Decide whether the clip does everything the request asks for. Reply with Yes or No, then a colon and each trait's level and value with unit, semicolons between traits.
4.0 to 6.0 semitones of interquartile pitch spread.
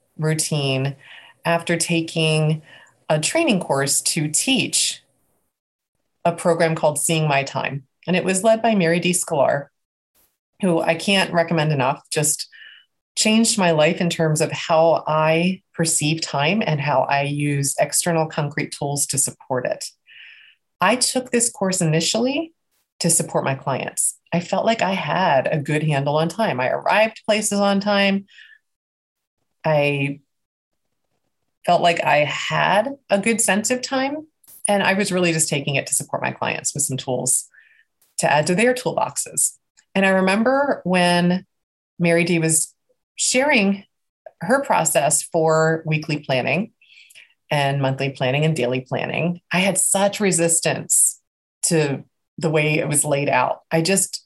Yes: average, 4.3 semitones